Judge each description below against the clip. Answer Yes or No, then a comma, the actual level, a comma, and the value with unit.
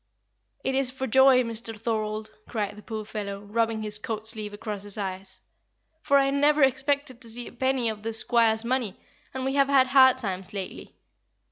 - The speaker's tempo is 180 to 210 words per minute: Yes, average, 190 wpm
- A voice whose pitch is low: No, high, 230 Hz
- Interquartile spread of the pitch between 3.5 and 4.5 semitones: Yes, average, 3.8 semitones